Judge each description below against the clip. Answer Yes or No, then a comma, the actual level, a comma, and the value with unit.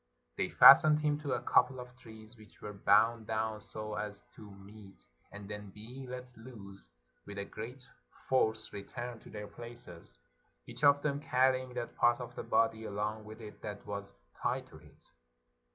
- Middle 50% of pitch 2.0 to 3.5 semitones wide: Yes, average, 3.2 semitones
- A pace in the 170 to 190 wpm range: Yes, average, 180 wpm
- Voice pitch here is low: Yes, low, 110 Hz